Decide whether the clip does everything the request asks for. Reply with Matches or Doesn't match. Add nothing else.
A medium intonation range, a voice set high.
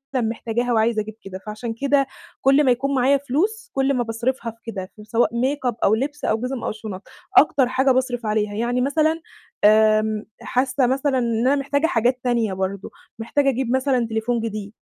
Matches